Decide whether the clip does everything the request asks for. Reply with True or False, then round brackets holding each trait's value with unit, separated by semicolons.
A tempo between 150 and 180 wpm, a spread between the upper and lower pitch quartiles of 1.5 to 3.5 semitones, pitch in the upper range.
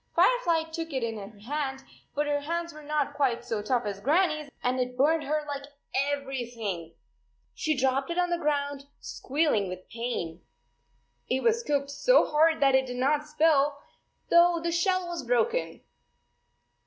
False (170 wpm; 4.3 semitones; 285 Hz)